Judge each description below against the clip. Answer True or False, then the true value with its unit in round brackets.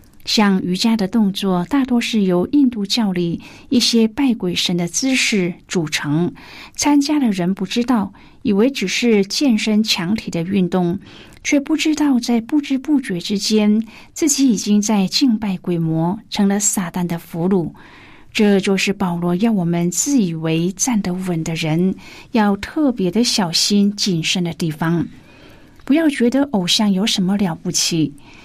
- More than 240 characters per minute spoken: False (230 characters per minute)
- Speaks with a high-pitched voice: True (205 Hz)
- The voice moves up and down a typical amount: True (4.8 semitones)